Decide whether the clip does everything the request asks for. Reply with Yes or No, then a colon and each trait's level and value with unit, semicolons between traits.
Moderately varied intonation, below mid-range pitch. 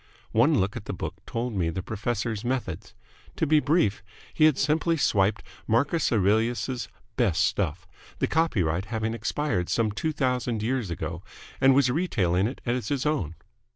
No: wide, 5.7 semitones; low, 115 Hz